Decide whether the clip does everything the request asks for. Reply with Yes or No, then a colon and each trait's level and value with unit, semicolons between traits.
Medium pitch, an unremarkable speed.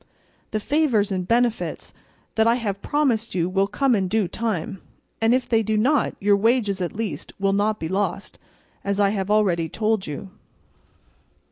No: high, 210 Hz; average, 170 wpm